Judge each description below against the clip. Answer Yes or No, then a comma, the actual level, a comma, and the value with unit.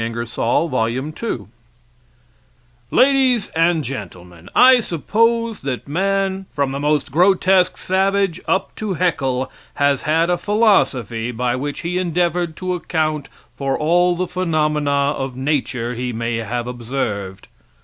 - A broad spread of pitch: Yes, wide, 6.5 semitones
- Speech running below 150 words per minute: Yes, slow, 135 wpm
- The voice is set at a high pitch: No, medium, 150 Hz